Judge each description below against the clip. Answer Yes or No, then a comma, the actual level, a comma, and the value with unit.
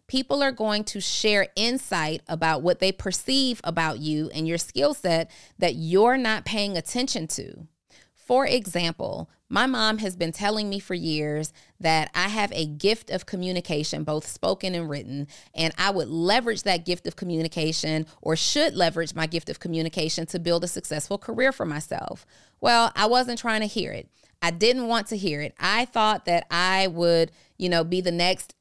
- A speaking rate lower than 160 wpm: No, average, 185 wpm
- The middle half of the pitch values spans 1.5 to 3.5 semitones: No, average, 4.8 semitones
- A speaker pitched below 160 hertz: No, medium, 180 Hz